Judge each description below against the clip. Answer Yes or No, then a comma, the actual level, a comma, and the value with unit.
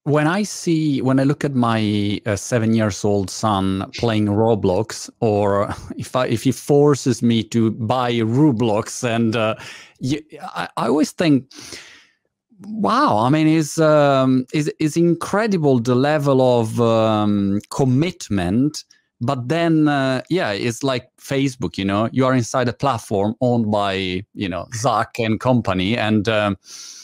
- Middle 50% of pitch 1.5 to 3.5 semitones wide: No, average, 4.9 semitones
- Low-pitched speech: Yes, low, 125 Hz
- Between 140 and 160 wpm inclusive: Yes, average, 150 wpm